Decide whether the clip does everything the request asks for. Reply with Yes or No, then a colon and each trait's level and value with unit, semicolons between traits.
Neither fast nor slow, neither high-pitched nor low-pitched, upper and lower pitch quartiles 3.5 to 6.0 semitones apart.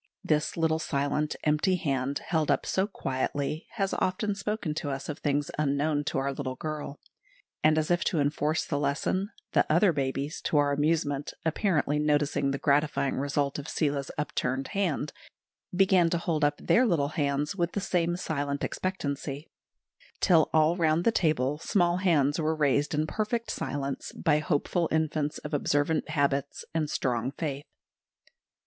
No: average, 160 wpm; medium, 150 Hz; average, 2.8 semitones